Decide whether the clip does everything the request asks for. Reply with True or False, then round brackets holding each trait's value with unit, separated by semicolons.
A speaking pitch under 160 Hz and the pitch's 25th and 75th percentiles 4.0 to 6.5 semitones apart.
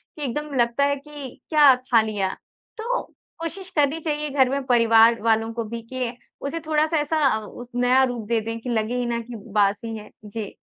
False (245 Hz; 4.3 semitones)